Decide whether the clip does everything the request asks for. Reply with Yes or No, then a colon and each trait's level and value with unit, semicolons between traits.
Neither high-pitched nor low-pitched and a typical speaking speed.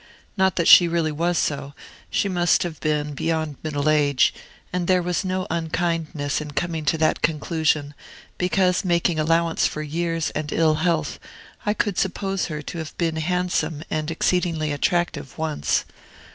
Yes: medium, 165 Hz; average, 160 wpm